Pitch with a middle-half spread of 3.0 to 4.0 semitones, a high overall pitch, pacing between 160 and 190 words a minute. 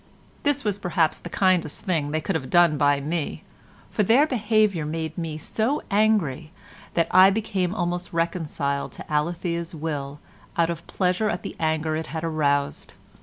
No: average, 3.5 semitones; medium, 170 Hz; average, 165 wpm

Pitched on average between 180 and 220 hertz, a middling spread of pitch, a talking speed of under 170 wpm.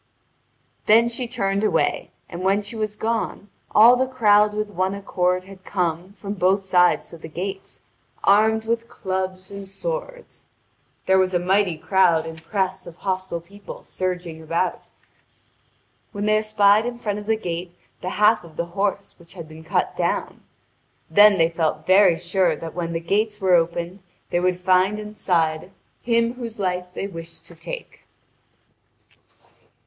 Yes: high, 190 Hz; average, 3.2 semitones; average, 160 wpm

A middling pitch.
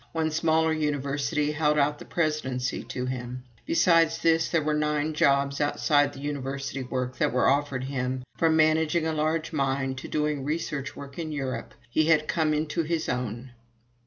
Yes: medium, 145 Hz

